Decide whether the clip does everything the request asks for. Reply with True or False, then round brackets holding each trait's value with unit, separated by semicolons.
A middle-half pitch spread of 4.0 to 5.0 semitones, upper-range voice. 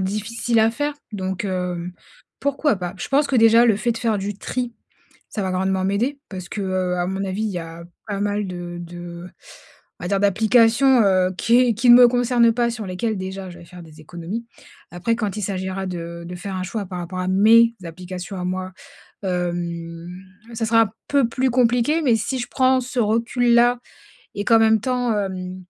True (4.3 semitones; 200 Hz)